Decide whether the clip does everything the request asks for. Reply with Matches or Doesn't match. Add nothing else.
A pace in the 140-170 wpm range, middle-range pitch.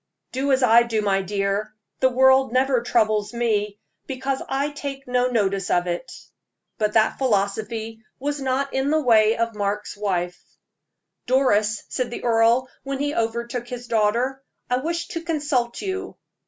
Doesn't match